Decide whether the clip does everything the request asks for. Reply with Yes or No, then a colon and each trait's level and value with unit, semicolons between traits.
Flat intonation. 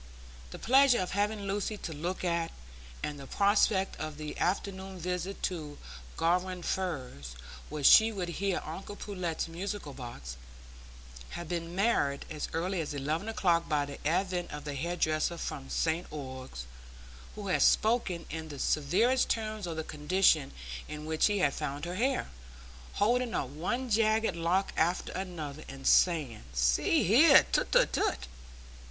No: average, 4.7 semitones